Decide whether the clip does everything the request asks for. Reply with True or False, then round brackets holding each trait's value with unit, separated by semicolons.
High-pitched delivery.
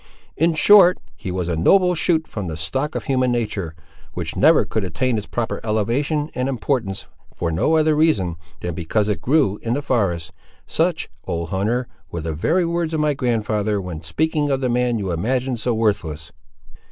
False (115 Hz)